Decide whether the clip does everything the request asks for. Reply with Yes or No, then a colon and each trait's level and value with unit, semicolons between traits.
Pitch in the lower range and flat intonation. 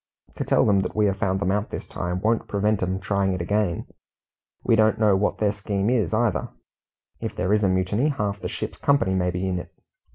Yes: low, 100 Hz; narrow, 2.2 semitones